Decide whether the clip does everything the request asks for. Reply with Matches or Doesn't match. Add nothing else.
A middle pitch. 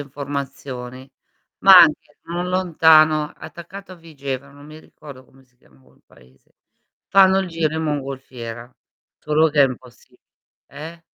Matches